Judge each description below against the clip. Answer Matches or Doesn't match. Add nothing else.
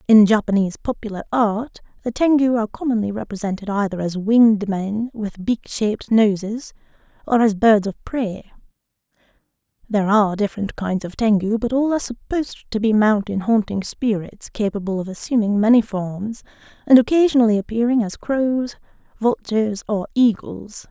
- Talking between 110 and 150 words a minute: Matches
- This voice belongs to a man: Doesn't match